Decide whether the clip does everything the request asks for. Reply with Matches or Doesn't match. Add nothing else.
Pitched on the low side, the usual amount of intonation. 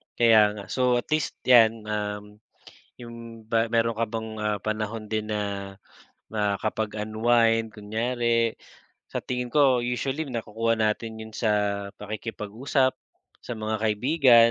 Doesn't match